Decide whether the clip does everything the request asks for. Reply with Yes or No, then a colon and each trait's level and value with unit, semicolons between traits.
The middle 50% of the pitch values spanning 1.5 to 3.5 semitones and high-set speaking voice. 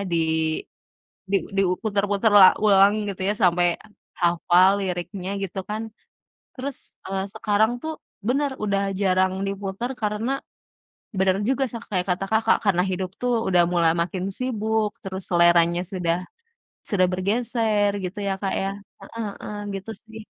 Yes: average, 2.8 semitones; high, 195 Hz